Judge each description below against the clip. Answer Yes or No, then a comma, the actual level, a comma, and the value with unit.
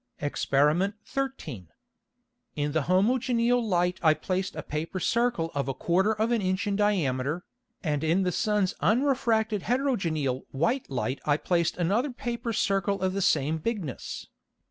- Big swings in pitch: Yes, wide, 6.5 semitones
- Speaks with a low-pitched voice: No, medium, 185 Hz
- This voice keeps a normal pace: Yes, average, 145 wpm